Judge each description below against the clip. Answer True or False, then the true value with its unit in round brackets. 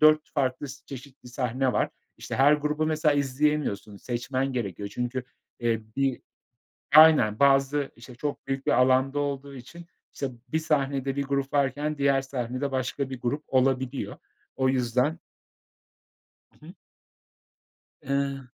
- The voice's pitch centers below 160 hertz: True (135 Hz)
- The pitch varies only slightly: True (1.9 semitones)